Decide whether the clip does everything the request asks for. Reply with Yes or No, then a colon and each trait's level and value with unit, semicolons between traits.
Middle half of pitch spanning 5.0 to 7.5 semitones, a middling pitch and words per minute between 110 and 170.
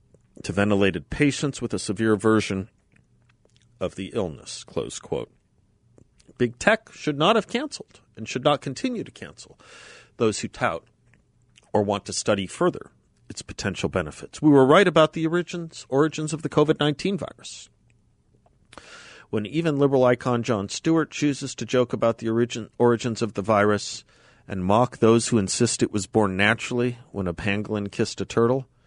No: average, 5.3 semitones; low, 120 Hz; average, 160 wpm